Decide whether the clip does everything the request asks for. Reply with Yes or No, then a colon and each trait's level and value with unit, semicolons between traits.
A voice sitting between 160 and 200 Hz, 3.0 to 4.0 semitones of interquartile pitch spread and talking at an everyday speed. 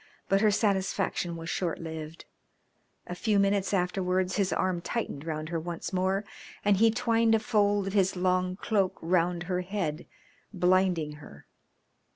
No: medium, 185 Hz; narrow, 2.6 semitones; average, 155 wpm